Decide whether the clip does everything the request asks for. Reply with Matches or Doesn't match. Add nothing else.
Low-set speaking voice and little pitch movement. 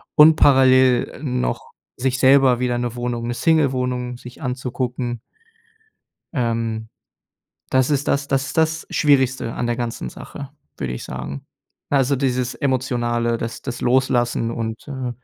Matches